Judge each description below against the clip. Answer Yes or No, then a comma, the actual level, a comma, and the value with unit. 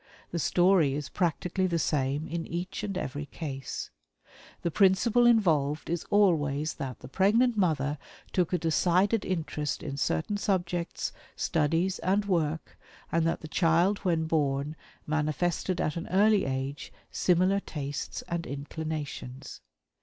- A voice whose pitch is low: No, medium, 165 Hz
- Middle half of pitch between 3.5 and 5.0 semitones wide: Yes, average, 4.0 semitones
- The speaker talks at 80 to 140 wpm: Yes, slow, 135 wpm